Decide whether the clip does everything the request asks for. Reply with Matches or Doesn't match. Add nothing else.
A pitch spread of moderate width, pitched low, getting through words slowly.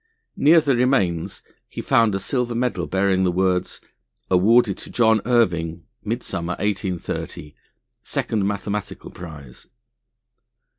Matches